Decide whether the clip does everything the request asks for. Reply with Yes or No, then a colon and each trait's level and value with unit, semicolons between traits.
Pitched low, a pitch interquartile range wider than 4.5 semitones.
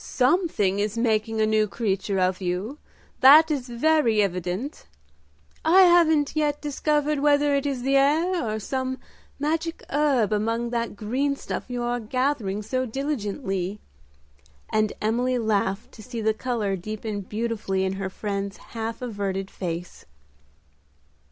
No: high, 230 Hz; wide, 5.4 semitones